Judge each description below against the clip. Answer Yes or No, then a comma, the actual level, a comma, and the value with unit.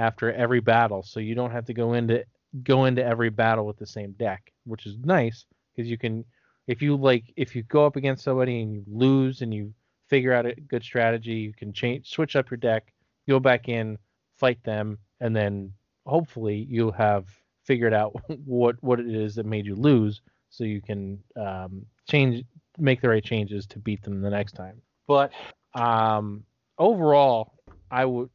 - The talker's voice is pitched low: Yes, low, 115 Hz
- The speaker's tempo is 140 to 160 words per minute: No, average, 190 wpm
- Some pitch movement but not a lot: Yes, average, 3.2 semitones